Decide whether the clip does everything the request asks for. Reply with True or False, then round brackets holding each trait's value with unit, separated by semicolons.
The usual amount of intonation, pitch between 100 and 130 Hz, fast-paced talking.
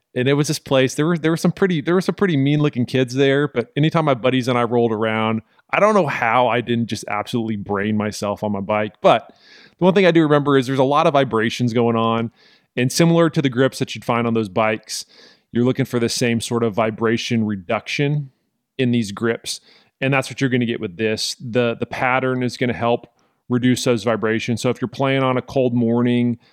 True (3.0 semitones; 125 Hz; 235 wpm)